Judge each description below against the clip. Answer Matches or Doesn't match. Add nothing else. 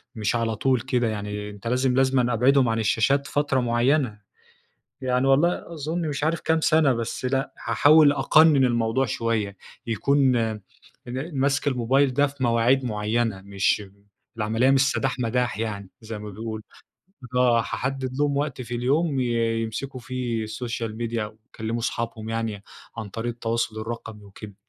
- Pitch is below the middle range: Matches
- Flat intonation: Doesn't match